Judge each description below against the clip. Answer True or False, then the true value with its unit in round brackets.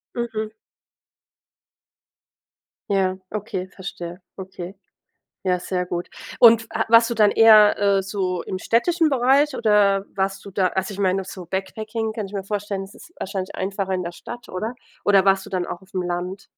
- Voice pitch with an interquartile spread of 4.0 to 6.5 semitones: False (2.6 semitones)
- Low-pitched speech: False (195 Hz)